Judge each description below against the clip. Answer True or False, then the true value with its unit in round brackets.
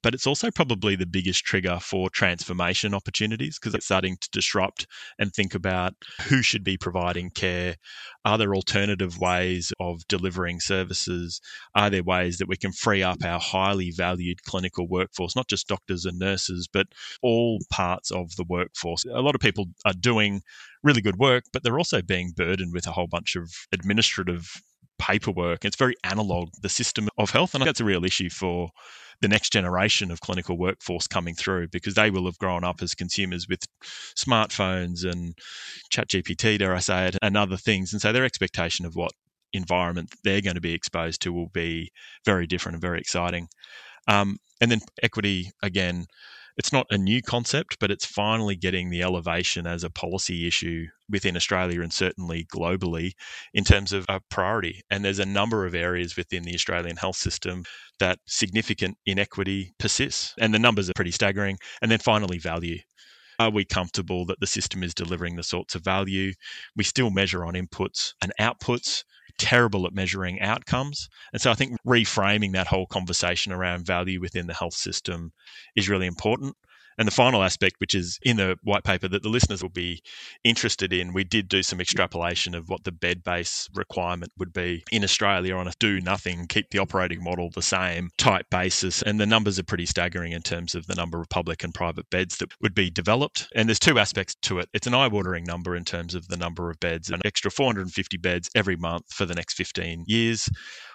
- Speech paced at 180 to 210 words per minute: True (195 wpm)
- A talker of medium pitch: False (95 Hz)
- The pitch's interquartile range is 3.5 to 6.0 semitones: False (2.8 semitones)